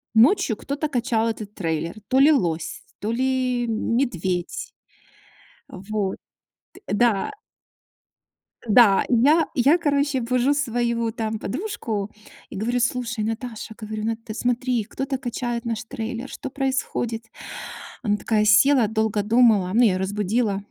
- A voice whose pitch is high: Yes, high, 230 Hz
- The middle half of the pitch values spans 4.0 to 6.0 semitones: No, average, 3.3 semitones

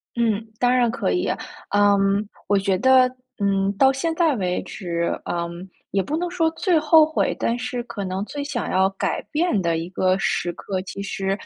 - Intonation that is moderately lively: No, wide, 5.8 semitones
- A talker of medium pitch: No, high, 205 Hz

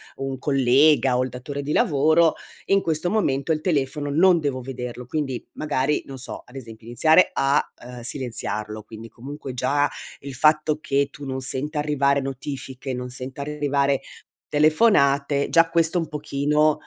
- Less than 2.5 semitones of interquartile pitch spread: No, average, 2.8 semitones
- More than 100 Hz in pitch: Yes, medium, 140 Hz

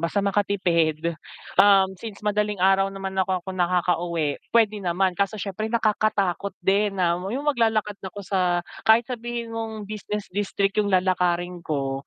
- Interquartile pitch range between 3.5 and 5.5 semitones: No, average, 2.8 semitones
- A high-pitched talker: Yes, high, 195 Hz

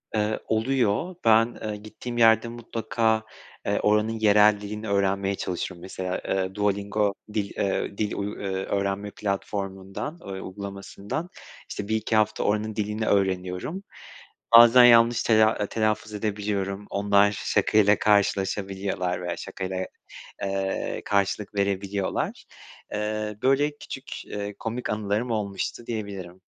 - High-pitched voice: No, low, 105 Hz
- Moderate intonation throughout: No, narrow, 1.8 semitones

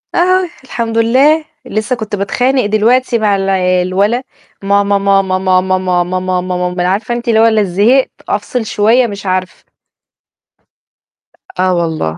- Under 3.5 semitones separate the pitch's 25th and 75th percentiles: No, average, 4.2 semitones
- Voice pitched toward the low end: No, high, 205 Hz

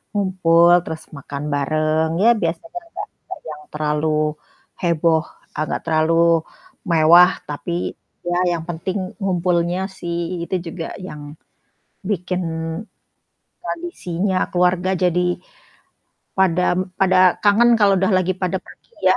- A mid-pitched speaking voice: Yes, medium, 175 Hz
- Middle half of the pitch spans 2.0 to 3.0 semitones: Yes, narrow, 2.6 semitones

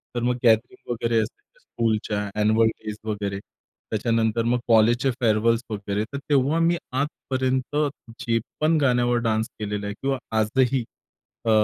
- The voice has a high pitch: No, low, 115 Hz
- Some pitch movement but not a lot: Yes, average, 3.0 semitones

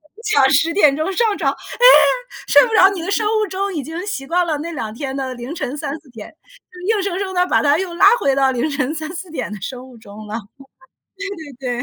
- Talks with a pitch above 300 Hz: Yes, very high, 310 Hz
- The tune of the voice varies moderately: No, wide, 6.1 semitones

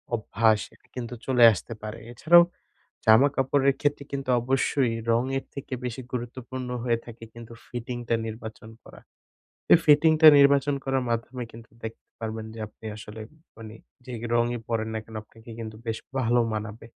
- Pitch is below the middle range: Yes, low, 120 Hz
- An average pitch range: Yes, average, 3.0 semitones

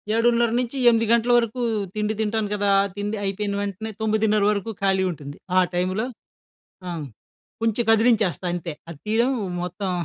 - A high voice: Yes, high, 210 Hz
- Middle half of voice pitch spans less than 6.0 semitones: Yes, narrow, 2.6 semitones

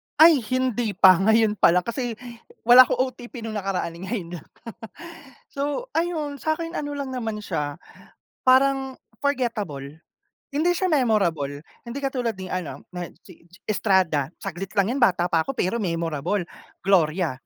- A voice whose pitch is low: No, high, 215 Hz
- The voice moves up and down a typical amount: No, wide, 6.9 semitones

